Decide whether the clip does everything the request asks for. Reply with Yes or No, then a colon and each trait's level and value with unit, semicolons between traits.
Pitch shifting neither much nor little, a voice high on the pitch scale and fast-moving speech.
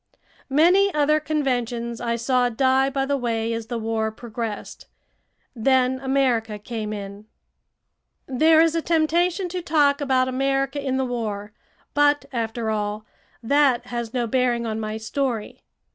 No: average, 3.9 semitones; very high, 250 Hz; average, 145 wpm